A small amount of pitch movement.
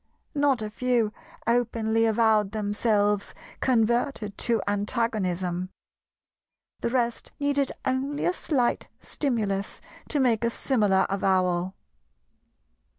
No: average, 3.5 semitones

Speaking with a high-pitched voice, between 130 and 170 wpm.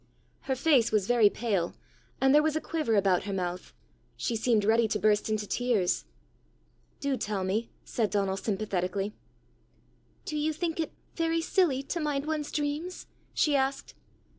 Yes: high, 235 Hz; average, 160 wpm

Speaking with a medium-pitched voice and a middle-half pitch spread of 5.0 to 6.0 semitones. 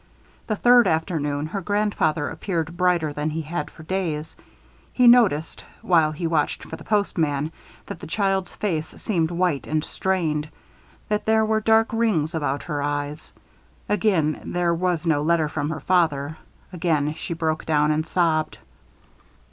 No: medium, 165 Hz; average, 3.7 semitones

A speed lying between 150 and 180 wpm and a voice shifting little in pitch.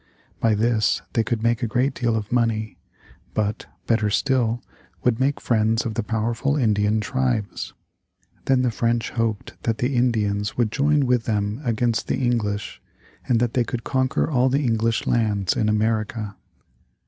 Yes: average, 160 wpm; narrow, 2.3 semitones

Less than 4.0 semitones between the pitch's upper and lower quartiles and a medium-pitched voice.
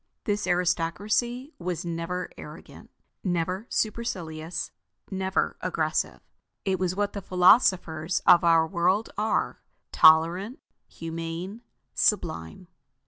Yes: average, 3.4 semitones; medium, 180 Hz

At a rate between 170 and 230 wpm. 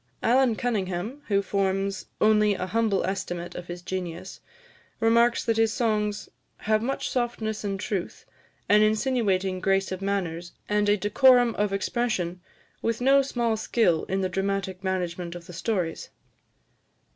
No: average, 145 wpm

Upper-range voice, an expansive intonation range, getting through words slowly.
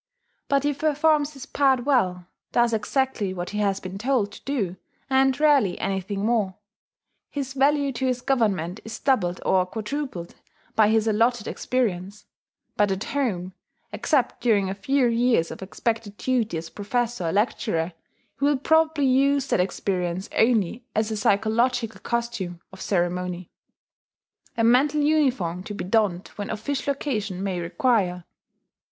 No: high, 225 Hz; wide, 5.7 semitones; average, 145 wpm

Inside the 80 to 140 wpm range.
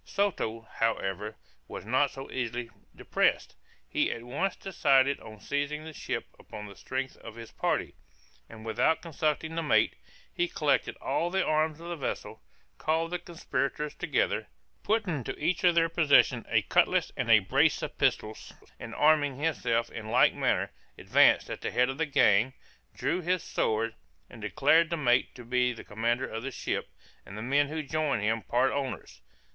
No: average, 175 wpm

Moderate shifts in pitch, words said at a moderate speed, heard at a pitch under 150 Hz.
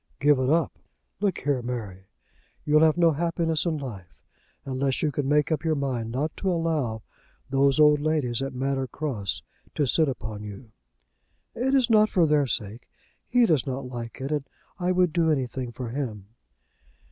Yes: average, 4.2 semitones; average, 175 wpm; medium, 140 Hz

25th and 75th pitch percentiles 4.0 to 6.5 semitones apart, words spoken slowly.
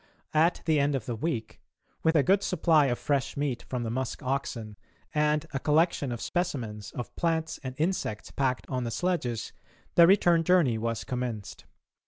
No: average, 5.3 semitones; average, 175 wpm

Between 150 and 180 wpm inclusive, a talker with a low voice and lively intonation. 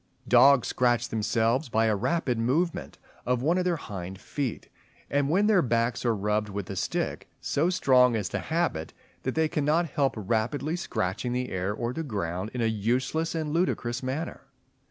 Yes: average, 175 wpm; low, 125 Hz; wide, 5.9 semitones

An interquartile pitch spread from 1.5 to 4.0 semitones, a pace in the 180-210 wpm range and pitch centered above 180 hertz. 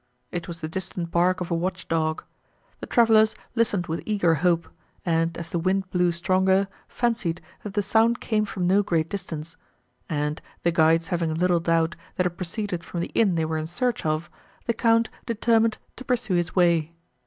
No: average, 3.7 semitones; average, 190 wpm; medium, 175 Hz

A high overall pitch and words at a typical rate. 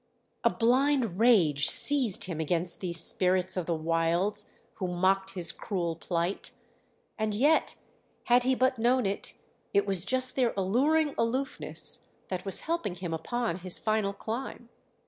Yes: high, 200 Hz; average, 145 wpm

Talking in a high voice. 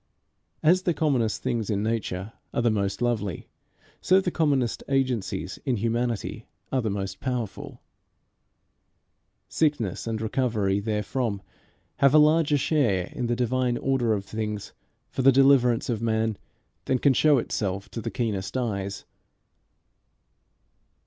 No: low, 115 Hz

